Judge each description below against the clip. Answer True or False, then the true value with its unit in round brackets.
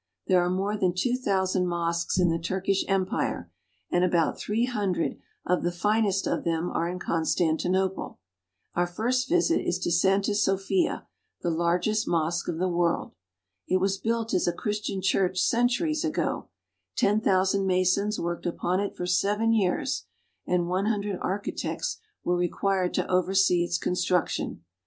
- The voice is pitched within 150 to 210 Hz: True (185 Hz)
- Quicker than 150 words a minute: True (160 wpm)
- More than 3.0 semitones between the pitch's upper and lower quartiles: False (2.7 semitones)